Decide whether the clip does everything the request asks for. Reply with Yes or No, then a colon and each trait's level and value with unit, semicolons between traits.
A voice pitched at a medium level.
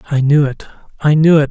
Yes: medium, 145 Hz